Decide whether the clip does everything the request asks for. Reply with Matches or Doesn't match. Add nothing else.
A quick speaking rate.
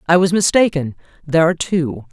Doesn't match